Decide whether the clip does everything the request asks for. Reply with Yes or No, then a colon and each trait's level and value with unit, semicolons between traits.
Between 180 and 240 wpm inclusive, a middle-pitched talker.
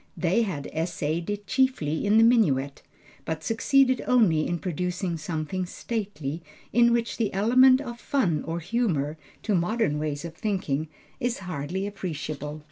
No: average, 145 wpm; medium, 180 Hz